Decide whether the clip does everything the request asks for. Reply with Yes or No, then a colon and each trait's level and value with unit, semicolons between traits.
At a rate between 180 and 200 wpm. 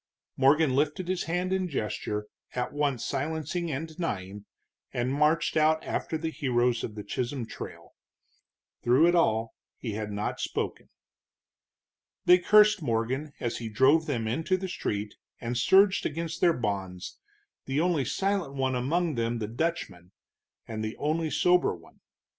No: average, 150 wpm